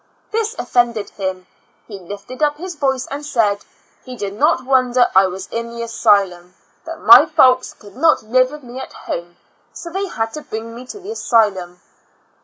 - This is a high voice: Yes, high, 240 Hz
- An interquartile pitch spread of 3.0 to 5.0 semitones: No, wide, 5.5 semitones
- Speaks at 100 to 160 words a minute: No, average, 190 wpm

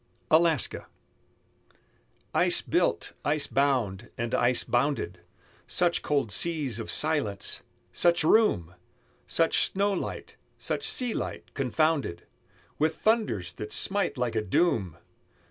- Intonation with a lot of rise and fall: Yes, wide, 6.7 semitones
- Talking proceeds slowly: Yes, slow, 110 wpm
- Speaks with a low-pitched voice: No, medium, 145 Hz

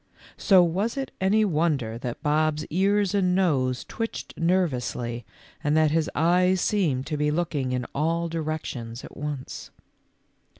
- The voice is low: No, medium, 155 Hz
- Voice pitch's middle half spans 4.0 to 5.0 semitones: Yes, average, 4.7 semitones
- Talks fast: No, average, 145 wpm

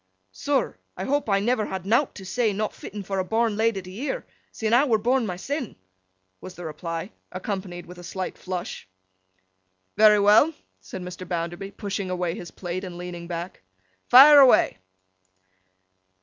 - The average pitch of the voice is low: No, high, 195 Hz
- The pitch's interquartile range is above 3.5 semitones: Yes, average, 4.1 semitones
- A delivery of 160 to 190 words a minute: Yes, average, 165 wpm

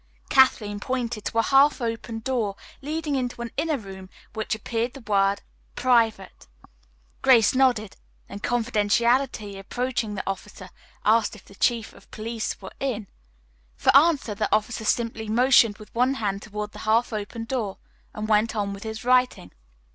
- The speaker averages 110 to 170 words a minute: Yes, average, 160 wpm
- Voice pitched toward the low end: No, high, 225 Hz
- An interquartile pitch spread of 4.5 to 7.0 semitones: No, average, 3.1 semitones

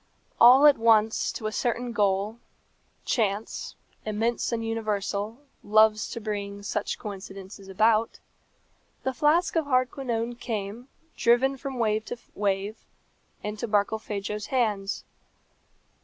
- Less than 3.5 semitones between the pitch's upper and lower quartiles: Yes, narrow, 2.6 semitones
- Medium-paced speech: No, slow, 110 wpm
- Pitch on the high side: Yes, high, 220 Hz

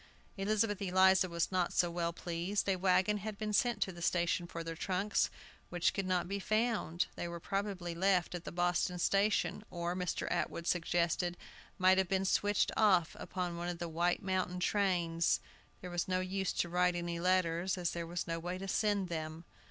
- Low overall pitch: No, medium, 180 Hz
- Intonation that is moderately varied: No, narrow, 2.1 semitones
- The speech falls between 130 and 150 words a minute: No, average, 190 wpm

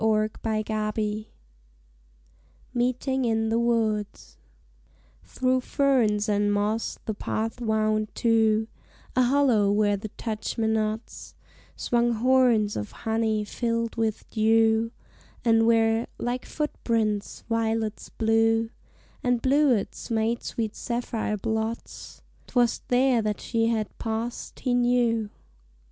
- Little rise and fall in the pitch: Yes, narrow, 1.7 semitones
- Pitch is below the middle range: No, high, 225 Hz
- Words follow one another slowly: Yes, slow, 115 wpm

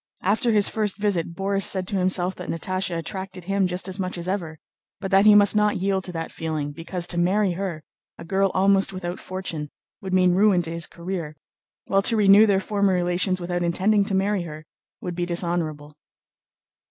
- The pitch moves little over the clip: Yes, narrow, 2.3 semitones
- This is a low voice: No, medium, 185 Hz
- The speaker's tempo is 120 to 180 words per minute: No, average, 195 wpm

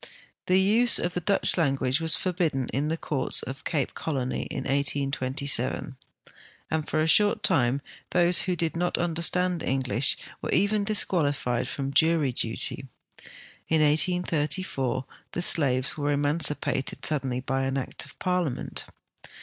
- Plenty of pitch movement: No, average, 4.5 semitones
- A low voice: No, medium, 150 Hz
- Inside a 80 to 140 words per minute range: Yes, slow, 135 wpm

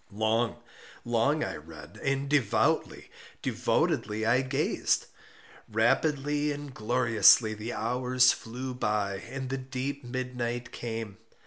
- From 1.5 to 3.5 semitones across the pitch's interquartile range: Yes, average, 3.1 semitones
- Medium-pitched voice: No, low, 120 Hz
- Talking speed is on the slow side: Yes, slow, 105 wpm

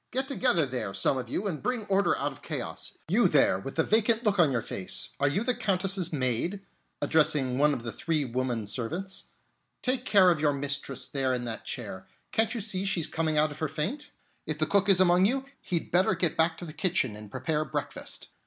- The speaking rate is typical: No, fast, 220 wpm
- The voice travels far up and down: Yes, wide, 6.6 semitones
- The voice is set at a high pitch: No, medium, 160 Hz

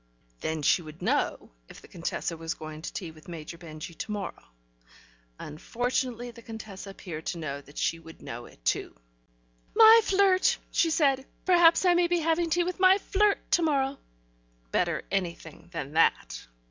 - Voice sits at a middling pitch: No, high, 205 Hz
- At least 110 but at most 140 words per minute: No, average, 170 wpm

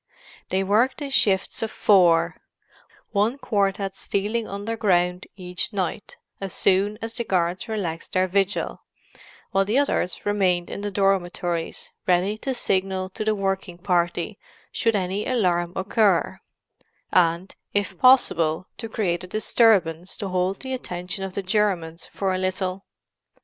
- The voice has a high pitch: Yes, high, 195 Hz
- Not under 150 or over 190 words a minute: No, average, 140 wpm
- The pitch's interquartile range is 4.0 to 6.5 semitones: No, average, 2.7 semitones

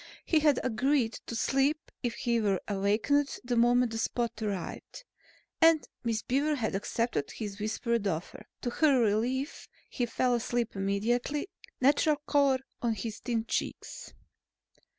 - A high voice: Yes, high, 240 Hz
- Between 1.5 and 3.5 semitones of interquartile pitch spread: No, average, 3.9 semitones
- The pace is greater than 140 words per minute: No, slow, 135 wpm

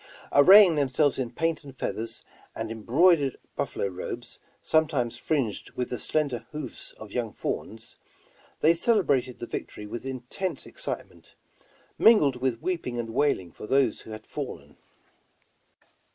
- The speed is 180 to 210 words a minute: No, average, 140 wpm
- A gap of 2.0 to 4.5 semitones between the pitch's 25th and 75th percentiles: No, average, 5.2 semitones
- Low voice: Yes, low, 130 Hz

